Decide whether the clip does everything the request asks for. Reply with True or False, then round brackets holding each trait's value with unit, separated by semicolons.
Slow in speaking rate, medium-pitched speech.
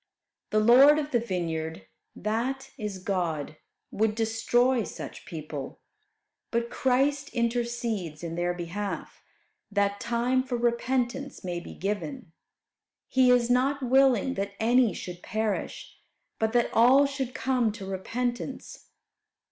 False (125 wpm; 235 Hz)